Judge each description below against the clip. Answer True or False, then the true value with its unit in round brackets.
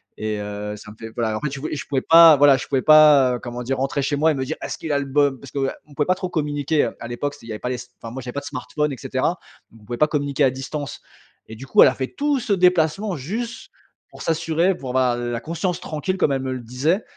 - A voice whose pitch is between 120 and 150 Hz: True (140 Hz)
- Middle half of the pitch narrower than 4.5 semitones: True (3.8 semitones)